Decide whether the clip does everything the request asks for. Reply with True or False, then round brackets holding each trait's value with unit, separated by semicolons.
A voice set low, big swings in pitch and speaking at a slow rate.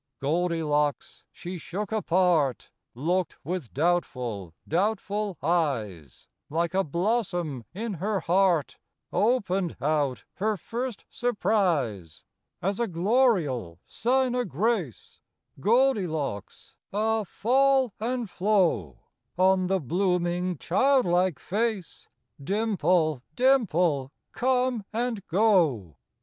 False (180 Hz; 6.1 semitones; 95 wpm)